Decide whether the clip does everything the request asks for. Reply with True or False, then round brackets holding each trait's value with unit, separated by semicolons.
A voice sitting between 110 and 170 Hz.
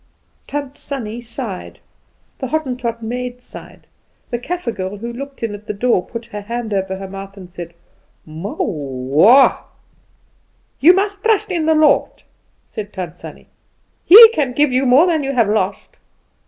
False (235 Hz)